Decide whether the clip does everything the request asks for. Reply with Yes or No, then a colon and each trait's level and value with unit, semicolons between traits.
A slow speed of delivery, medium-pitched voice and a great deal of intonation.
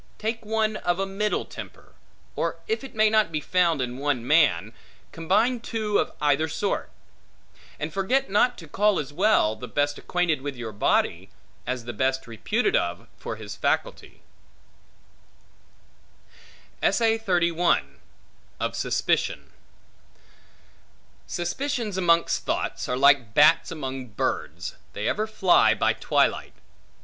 Yes: slow, 125 wpm; medium, 170 Hz; wide, 8.2 semitones